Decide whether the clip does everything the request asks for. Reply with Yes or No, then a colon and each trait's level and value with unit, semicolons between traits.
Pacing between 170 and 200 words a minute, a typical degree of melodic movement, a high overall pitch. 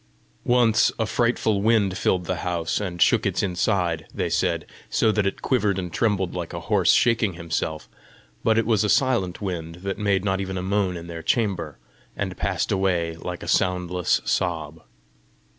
No: average, 175 wpm; average, 3.2 semitones; very low, 95 Hz